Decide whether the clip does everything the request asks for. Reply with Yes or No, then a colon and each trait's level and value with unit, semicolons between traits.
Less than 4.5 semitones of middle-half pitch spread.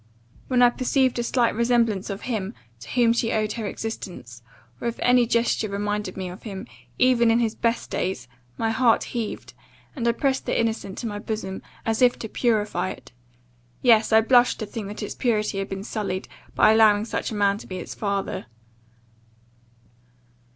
Yes: average, 2.8 semitones